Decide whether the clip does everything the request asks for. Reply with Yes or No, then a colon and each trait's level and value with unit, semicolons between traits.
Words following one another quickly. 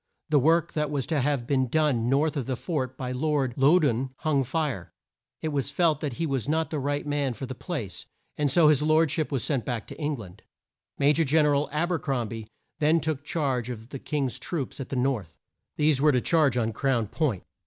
Yes: fast, 230 wpm